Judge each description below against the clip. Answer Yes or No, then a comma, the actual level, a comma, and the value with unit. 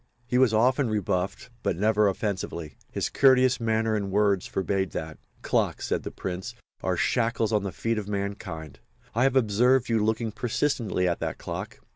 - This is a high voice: No, low, 105 Hz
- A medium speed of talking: Yes, average, 170 wpm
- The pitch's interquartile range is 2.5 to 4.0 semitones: Yes, average, 3.3 semitones